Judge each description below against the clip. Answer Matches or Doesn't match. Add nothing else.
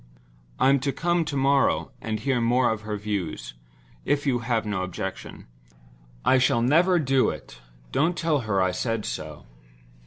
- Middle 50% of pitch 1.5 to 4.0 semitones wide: Doesn't match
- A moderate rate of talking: Matches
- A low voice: Matches